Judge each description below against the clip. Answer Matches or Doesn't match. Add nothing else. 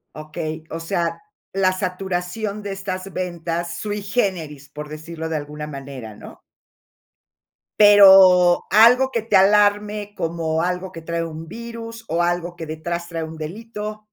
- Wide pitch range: Doesn't match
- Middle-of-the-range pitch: Matches